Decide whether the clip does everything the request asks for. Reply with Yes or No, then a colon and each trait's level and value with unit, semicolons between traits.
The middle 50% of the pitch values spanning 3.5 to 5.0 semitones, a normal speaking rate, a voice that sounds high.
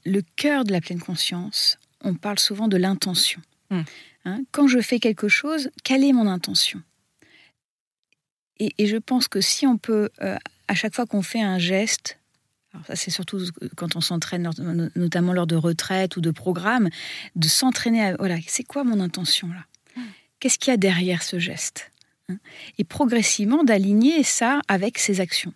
Yes: average, 4.7 semitones; average, 175 wpm; high, 195 Hz